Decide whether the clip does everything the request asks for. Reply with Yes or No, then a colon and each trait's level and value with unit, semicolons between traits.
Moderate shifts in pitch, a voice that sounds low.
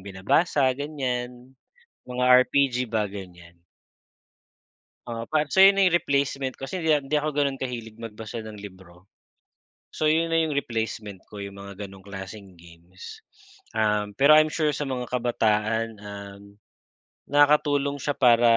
No: wide, 5.8 semitones; low, 120 Hz